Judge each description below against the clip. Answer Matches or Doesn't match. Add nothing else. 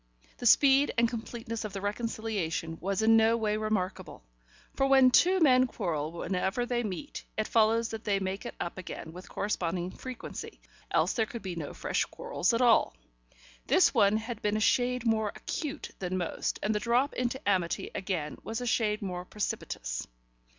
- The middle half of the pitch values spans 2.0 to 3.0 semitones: Doesn't match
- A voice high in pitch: Matches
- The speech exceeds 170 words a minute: Matches